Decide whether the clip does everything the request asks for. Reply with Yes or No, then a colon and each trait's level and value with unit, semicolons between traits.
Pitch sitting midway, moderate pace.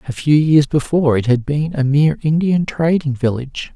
Yes: medium, 145 Hz; average, 190 wpm